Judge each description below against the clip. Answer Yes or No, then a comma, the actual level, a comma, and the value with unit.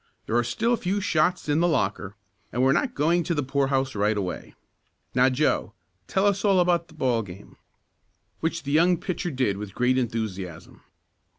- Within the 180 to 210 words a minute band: Yes, average, 185 wpm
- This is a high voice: No, low, 135 Hz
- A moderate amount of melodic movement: No, wide, 7.3 semitones